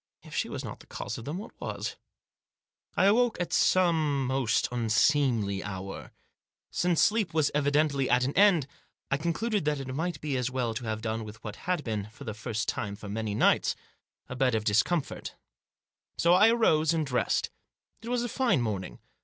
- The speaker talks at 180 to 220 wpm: Yes, average, 185 wpm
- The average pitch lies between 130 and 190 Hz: Yes, low, 135 Hz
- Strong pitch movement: Yes, wide, 7.4 semitones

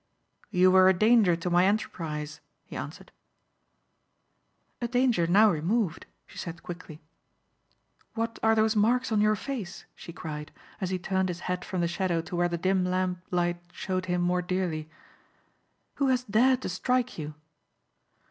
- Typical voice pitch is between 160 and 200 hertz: Yes, medium, 185 Hz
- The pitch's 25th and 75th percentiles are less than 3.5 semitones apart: No, average, 3.8 semitones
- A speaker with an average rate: Yes, average, 160 wpm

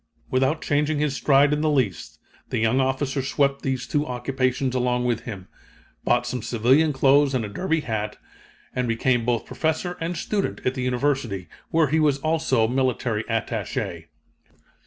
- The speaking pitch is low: Yes, low, 130 Hz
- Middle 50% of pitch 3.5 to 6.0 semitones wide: No, average, 3.1 semitones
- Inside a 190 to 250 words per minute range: No, average, 160 wpm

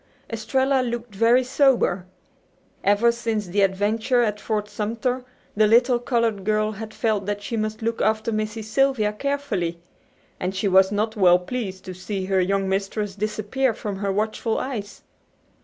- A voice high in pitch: Yes, high, 215 Hz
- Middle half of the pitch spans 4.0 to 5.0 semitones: No, average, 2.9 semitones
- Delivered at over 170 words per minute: No, average, 155 wpm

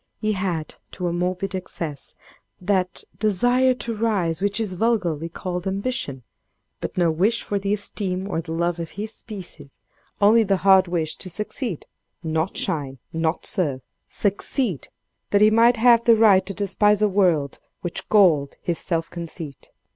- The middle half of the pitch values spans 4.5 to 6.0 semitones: No, average, 4.0 semitones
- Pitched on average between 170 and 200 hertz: Yes, high, 190 Hz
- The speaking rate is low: No, average, 155 wpm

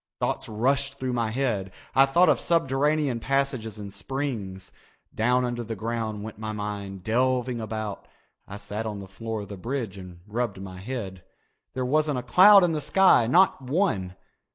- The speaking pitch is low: Yes, low, 115 Hz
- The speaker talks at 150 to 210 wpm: Yes, average, 175 wpm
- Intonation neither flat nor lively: Yes, average, 4.6 semitones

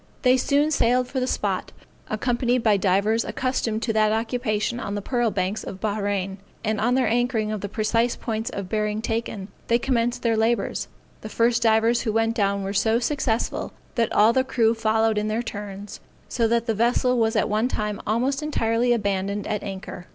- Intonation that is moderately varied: No, narrow, 2.3 semitones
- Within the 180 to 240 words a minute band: Yes, average, 190 wpm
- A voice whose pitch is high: Yes, high, 225 Hz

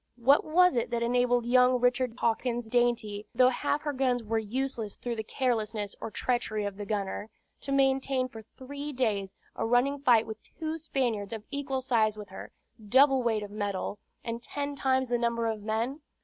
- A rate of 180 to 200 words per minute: Yes, average, 185 wpm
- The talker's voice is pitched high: Yes, high, 240 Hz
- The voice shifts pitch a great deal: No, average, 3.2 semitones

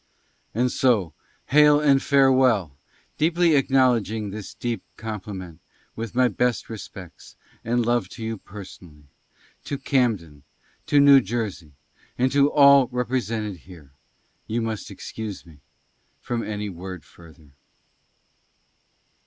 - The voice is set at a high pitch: No, low, 115 Hz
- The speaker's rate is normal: No, slow, 130 wpm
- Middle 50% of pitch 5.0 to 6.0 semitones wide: Yes, wide, 5.5 semitones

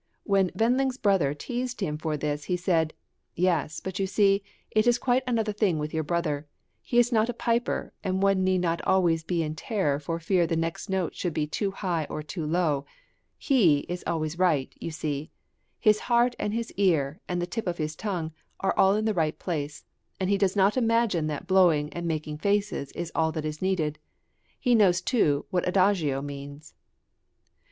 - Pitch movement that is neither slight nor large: Yes, average, 4.7 semitones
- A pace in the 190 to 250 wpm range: Yes, average, 195 wpm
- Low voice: No, medium, 180 Hz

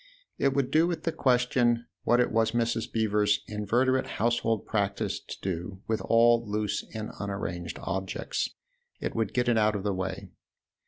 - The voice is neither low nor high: No, low, 110 Hz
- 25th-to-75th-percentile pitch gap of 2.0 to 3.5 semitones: Yes, average, 2.8 semitones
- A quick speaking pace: No, average, 165 wpm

